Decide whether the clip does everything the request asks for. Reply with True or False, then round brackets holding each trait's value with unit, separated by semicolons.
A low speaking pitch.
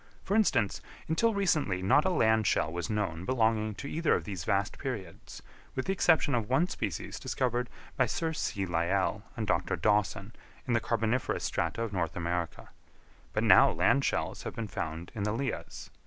True (110 Hz)